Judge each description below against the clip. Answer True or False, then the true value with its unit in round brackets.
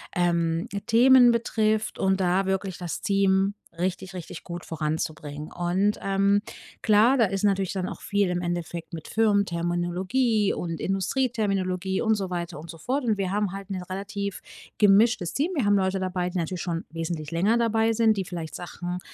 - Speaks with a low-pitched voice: False (190 Hz)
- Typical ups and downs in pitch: True (3.1 semitones)